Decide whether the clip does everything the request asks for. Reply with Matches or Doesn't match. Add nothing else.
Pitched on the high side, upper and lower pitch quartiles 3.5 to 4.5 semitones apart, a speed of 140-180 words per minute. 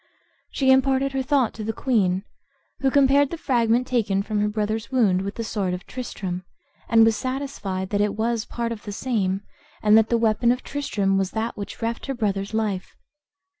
Doesn't match